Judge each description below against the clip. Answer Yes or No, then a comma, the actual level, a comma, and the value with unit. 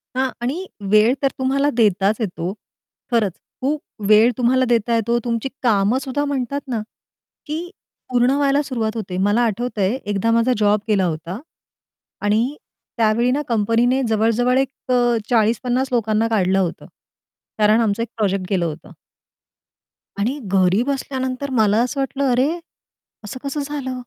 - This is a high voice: Yes, high, 230 Hz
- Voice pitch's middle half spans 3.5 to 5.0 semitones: Yes, average, 3.8 semitones